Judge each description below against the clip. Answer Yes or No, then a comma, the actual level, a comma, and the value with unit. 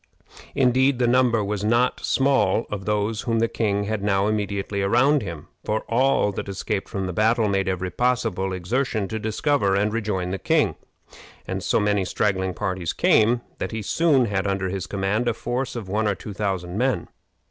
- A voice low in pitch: Yes, low, 105 Hz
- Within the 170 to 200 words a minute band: Yes, average, 185 wpm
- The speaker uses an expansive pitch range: No, average, 3.3 semitones